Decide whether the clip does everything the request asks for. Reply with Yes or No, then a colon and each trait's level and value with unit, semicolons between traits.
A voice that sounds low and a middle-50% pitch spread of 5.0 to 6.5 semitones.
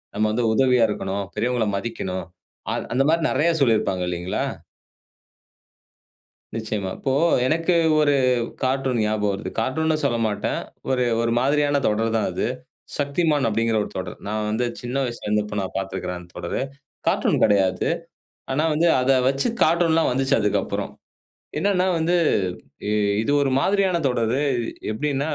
Yes: low, 125 Hz; average, 5.3 semitones